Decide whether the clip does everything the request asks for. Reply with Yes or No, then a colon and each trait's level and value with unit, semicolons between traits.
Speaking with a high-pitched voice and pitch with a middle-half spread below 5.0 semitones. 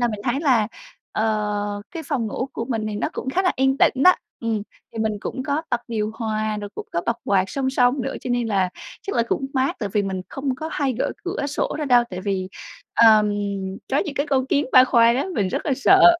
Yes: high, 240 Hz; average, 4.2 semitones